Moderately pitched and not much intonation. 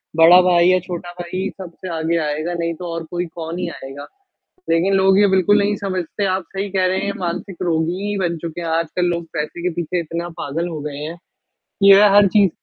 Yes: medium, 175 Hz; narrow, 2.3 semitones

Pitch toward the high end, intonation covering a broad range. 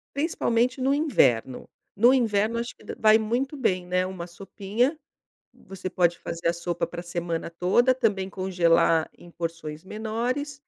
Yes: high, 195 Hz; wide, 5.8 semitones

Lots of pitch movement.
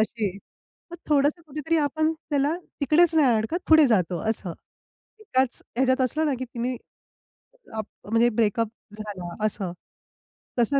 Yes: wide, 5.7 semitones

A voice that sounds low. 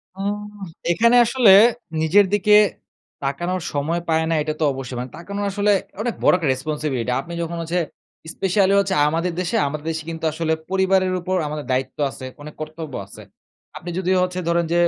No: medium, 170 Hz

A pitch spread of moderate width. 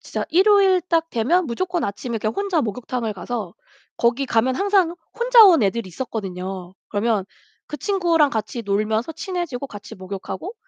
No: wide, 8.8 semitones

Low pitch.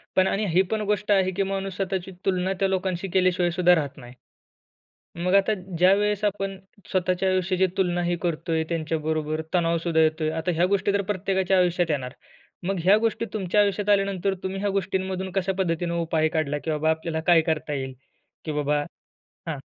No: medium, 180 Hz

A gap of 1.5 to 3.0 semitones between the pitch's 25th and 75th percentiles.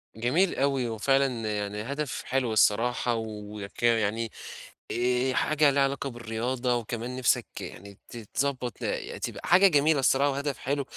No: average, 3.6 semitones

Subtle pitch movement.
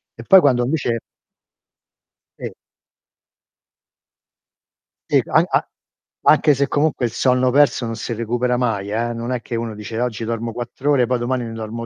Yes: narrow, 1.9 semitones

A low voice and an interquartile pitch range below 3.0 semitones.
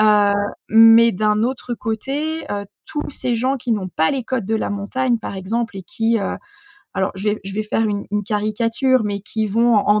No: high, 220 Hz; narrow, 2.6 semitones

